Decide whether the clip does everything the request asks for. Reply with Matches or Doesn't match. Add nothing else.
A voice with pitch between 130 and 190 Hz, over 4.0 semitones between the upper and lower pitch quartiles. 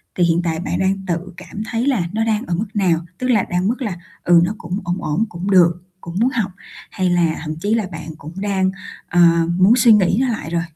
Doesn't match